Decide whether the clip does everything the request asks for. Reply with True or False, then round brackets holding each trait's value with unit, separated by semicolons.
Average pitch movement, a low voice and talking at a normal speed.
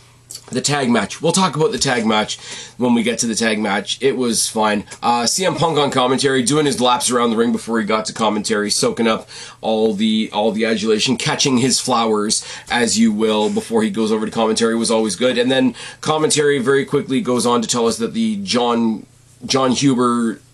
False (4.0 semitones; 125 Hz; 215 wpm)